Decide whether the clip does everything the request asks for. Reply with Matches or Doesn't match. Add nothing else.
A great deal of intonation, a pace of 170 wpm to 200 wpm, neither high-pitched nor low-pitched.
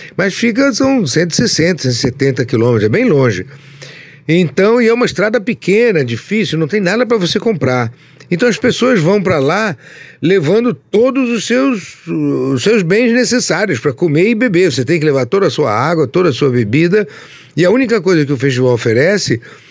Matches